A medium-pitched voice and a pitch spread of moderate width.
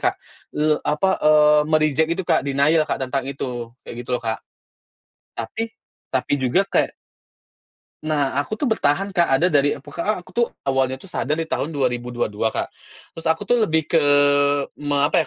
Yes: medium, 150 Hz; average, 3.6 semitones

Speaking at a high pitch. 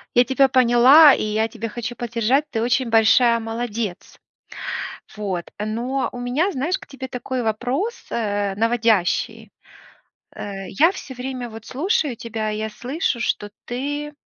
Yes: high, 240 Hz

